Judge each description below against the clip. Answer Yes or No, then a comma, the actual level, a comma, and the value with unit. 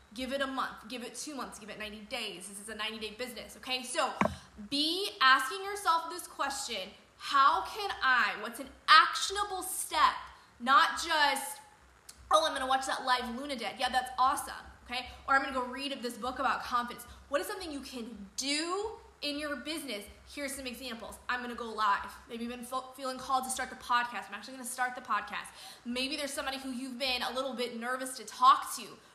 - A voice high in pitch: Yes, very high, 260 Hz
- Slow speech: No, fast, 205 wpm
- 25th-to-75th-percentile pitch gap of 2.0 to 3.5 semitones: Yes, average, 3.0 semitones